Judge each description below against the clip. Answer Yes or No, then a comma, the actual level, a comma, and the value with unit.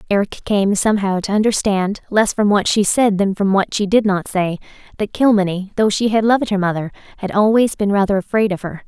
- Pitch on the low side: No, high, 200 Hz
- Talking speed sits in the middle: No, fast, 215 wpm